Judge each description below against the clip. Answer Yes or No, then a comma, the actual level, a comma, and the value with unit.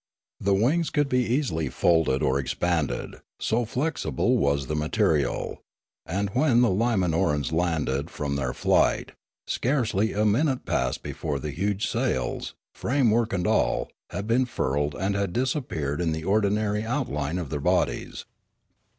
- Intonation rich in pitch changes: Yes, wide, 7.8 semitones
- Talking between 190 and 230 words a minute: No, average, 140 wpm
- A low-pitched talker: Yes, very low, 95 Hz